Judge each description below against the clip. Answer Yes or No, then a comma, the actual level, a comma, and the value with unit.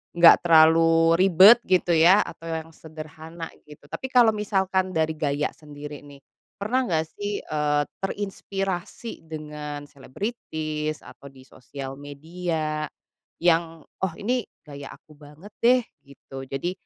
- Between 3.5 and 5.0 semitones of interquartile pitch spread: Yes, average, 4.0 semitones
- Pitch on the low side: No, medium, 160 Hz